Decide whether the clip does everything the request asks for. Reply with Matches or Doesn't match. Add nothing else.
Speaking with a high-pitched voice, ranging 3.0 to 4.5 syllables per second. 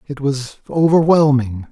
Doesn't match